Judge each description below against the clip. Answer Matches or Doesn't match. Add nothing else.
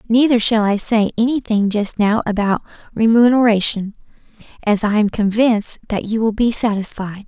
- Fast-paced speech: Doesn't match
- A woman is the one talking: Matches